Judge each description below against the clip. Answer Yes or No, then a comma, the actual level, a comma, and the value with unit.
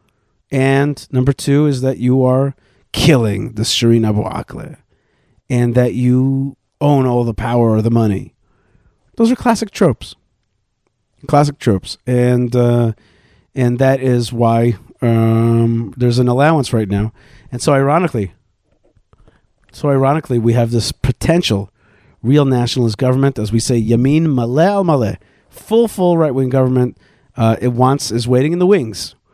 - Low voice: Yes, low, 125 Hz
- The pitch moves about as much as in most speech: Yes, average, 3.3 semitones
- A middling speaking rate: Yes, average, 145 wpm